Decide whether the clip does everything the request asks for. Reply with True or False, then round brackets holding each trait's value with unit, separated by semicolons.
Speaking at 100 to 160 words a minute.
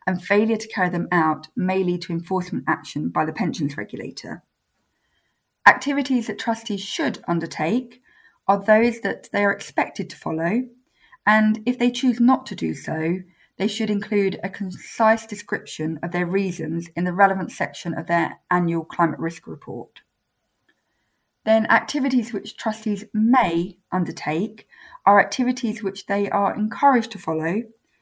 True (150 wpm)